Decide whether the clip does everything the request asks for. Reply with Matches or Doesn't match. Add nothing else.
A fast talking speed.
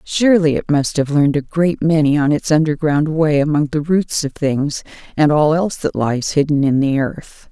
Matches